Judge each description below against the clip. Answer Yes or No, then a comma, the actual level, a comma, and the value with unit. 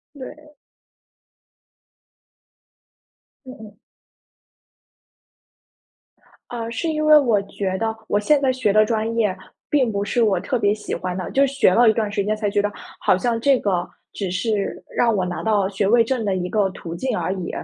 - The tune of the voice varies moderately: Yes, average, 3.5 semitones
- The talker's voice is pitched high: Yes, high, 215 Hz